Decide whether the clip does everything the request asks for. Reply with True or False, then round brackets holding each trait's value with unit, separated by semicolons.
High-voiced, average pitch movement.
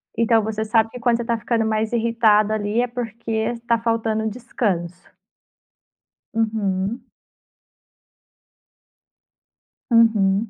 False (225 Hz; 1.4 semitones)